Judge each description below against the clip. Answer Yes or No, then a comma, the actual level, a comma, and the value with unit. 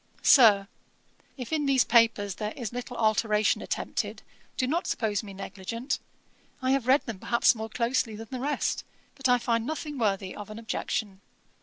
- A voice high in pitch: Yes, high, 230 Hz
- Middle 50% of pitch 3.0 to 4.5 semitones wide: Yes, average, 3.5 semitones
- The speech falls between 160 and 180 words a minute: Yes, average, 170 wpm